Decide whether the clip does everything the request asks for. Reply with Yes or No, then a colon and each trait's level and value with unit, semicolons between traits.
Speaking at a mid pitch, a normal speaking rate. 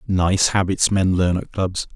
No: very low, 95 Hz; average, 185 wpm